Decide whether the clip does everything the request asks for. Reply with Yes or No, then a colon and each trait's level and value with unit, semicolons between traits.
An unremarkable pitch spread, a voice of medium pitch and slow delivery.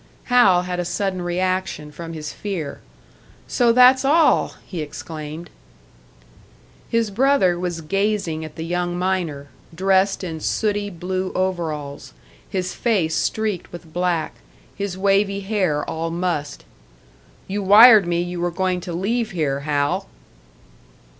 Yes: average, 3.3 semitones; medium, 180 Hz; slow, 130 wpm